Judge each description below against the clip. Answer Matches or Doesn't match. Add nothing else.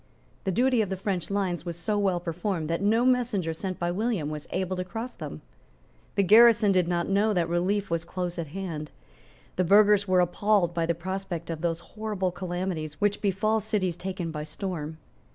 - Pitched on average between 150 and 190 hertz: Matches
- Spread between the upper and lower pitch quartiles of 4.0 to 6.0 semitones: Doesn't match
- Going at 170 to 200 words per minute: Matches